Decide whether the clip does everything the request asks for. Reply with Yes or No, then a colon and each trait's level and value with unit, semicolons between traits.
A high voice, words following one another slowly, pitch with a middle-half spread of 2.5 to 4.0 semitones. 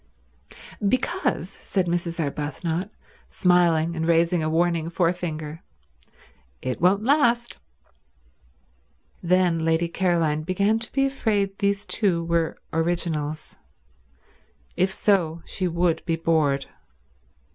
No: medium, 170 Hz; slow, 105 wpm; average, 2.9 semitones